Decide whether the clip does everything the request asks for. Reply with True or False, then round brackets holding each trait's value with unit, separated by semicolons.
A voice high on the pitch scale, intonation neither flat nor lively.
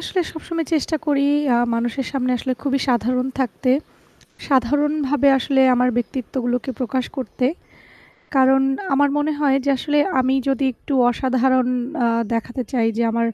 False (260 Hz; 2.3 semitones)